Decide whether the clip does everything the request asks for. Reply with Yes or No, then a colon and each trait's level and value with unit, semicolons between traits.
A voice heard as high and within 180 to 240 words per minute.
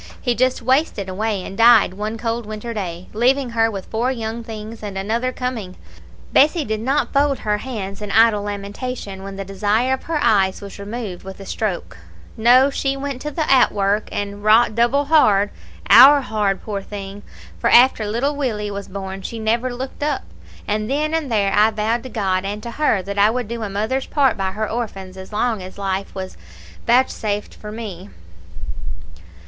Yes: high, 220 Hz; average, 185 wpm